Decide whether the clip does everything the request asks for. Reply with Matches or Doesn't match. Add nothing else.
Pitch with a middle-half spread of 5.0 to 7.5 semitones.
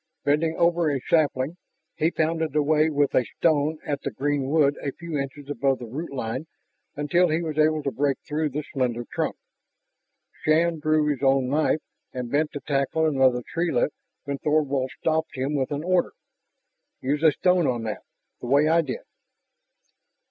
Doesn't match